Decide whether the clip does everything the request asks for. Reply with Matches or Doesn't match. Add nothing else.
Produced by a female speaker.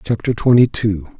Doesn't match